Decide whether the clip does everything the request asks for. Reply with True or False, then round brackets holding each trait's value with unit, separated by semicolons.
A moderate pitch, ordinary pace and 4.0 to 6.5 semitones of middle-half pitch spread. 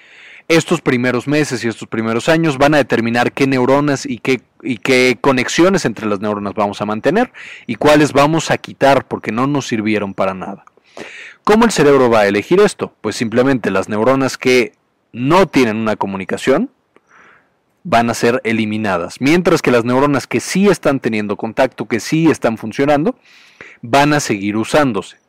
False (125 Hz; 170 wpm; 4.6 semitones)